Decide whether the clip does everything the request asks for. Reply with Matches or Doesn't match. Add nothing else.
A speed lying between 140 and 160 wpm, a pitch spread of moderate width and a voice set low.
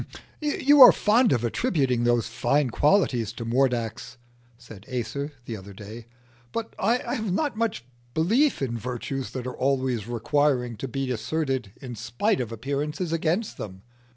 Doesn't match